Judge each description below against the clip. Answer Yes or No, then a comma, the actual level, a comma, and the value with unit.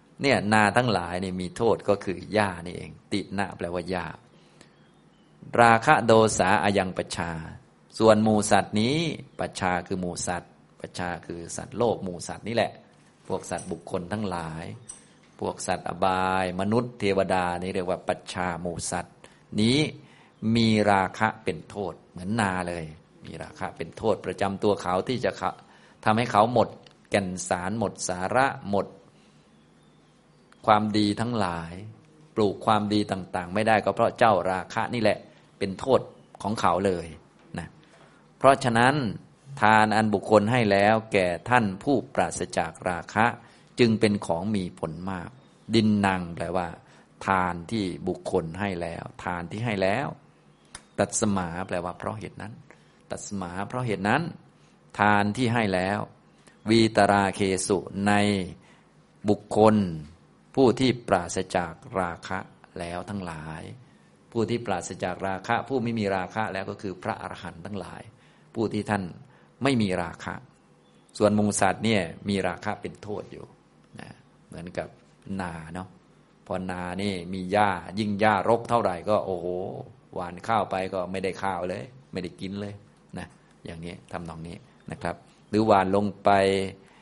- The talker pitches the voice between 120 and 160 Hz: No, low, 100 Hz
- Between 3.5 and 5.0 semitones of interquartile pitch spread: No, average, 3.1 semitones